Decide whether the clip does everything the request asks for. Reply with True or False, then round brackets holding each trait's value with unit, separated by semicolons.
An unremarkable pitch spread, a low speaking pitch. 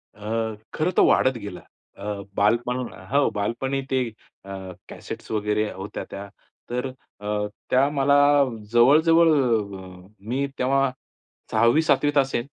True (4.6 semitones; 125 Hz)